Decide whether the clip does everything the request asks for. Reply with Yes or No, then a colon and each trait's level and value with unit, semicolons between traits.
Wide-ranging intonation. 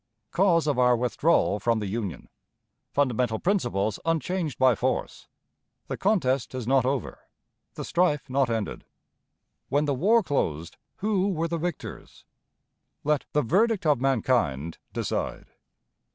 Yes: wide, 6.2 semitones